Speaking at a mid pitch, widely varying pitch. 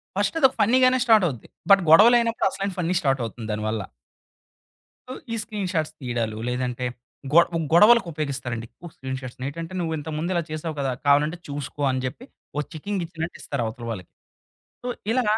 Yes: medium, 155 Hz; wide, 7.4 semitones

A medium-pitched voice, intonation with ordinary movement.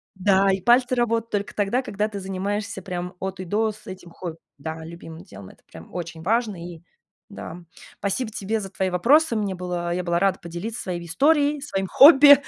No: high, 195 Hz; average, 4.2 semitones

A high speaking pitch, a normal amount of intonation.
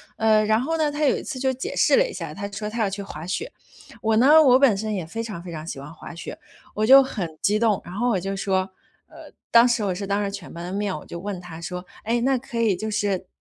Yes: high, 210 Hz; average, 4.2 semitones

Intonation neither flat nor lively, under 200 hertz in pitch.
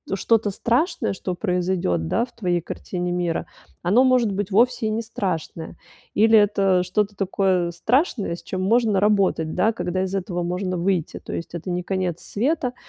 Yes: average, 3.6 semitones; high, 190 Hz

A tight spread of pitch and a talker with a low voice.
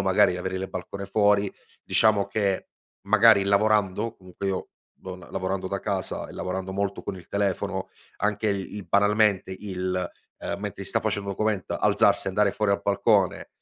Yes: narrow, 1.6 semitones; low, 100 Hz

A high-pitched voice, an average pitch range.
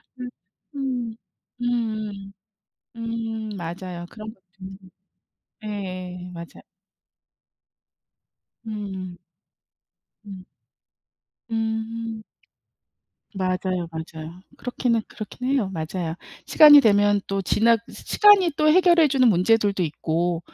Yes: high, 210 Hz; average, 4.0 semitones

